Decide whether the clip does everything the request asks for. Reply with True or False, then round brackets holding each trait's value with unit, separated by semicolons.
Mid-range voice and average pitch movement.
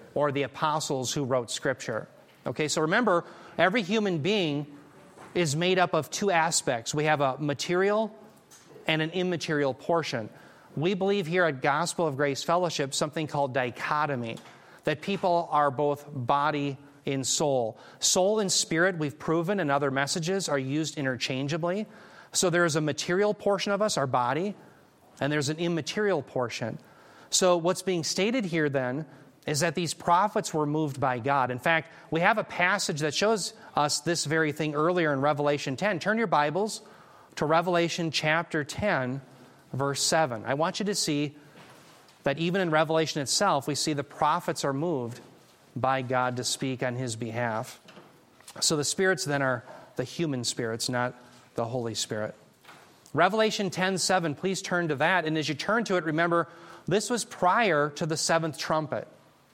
True (155 Hz; 4.2 semitones)